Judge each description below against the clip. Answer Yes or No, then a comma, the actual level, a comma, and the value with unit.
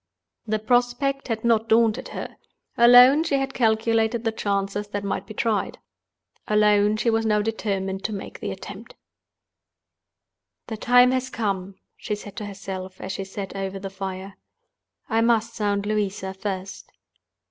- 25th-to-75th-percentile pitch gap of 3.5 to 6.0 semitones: No, narrow, 2.6 semitones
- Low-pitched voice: No, high, 210 Hz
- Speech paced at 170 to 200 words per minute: No, average, 150 wpm